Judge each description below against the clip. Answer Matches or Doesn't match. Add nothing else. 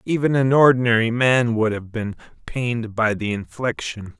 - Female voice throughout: Doesn't match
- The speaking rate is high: Doesn't match